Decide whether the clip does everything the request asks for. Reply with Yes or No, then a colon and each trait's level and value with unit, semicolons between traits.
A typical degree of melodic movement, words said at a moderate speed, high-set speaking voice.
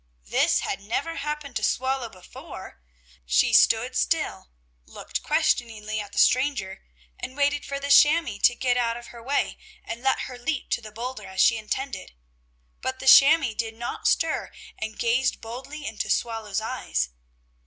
Yes: average, 4.1 semitones; average, 165 wpm; high, 240 Hz